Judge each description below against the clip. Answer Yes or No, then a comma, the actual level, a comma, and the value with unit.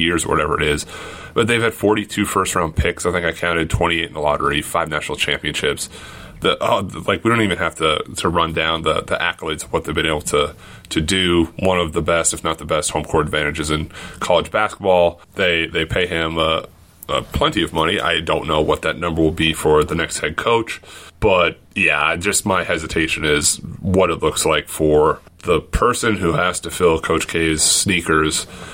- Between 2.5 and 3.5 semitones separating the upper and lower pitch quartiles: Yes, average, 2.9 semitones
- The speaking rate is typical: No, fast, 215 wpm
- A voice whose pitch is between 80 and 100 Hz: Yes, very low, 85 Hz